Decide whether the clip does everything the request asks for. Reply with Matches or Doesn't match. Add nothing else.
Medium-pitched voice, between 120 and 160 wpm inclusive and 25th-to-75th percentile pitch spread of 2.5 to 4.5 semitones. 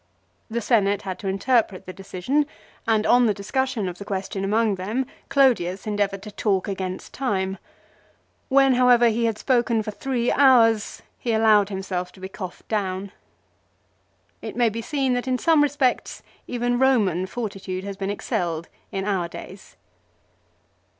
Doesn't match